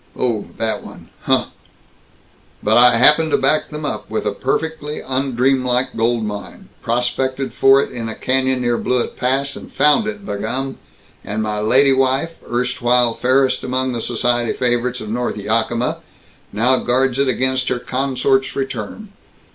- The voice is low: Yes, low, 125 Hz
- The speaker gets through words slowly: No, average, 155 wpm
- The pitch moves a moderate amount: No, narrow, 2.0 semitones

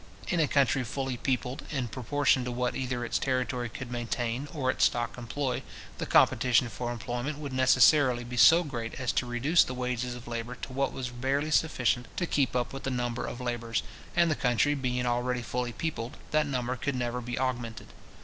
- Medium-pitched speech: No, low, 125 Hz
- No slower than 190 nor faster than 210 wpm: Yes, average, 195 wpm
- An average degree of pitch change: No, narrow, 2.0 semitones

